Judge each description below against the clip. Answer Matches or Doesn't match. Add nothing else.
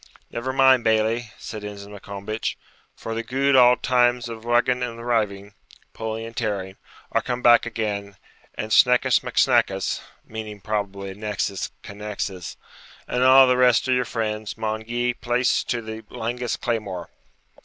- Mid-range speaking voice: Doesn't match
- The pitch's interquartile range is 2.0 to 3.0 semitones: Matches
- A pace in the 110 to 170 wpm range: Matches